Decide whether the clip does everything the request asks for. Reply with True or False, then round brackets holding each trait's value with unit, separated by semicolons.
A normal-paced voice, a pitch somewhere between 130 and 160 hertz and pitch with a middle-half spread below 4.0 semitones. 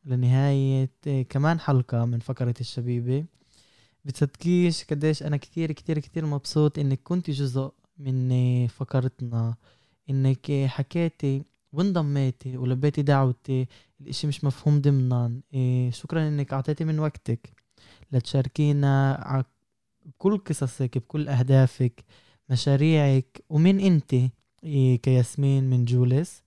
True (100 wpm; 135 Hz; 2.8 semitones)